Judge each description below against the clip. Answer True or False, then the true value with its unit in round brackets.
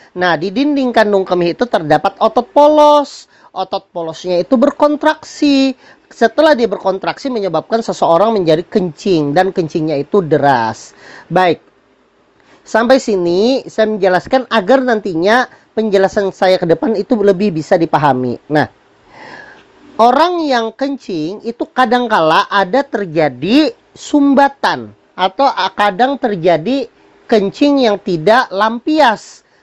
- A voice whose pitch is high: True (215 Hz)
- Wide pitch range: True (6.3 semitones)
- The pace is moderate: True (115 wpm)